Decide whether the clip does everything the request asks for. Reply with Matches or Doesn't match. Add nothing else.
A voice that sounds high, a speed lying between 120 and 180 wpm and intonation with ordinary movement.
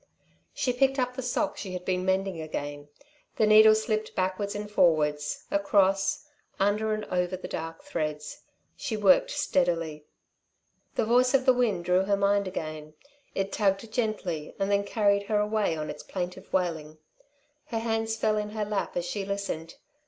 Matches